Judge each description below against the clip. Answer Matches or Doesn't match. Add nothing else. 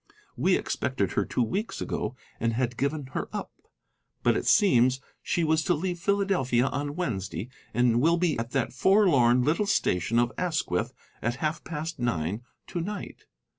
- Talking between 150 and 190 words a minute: Matches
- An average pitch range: Doesn't match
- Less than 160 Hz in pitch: Matches